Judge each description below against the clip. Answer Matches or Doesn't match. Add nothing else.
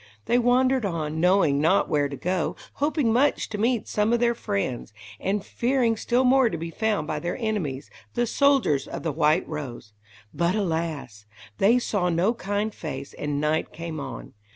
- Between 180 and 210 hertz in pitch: Matches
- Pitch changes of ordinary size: Doesn't match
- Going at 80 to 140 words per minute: Doesn't match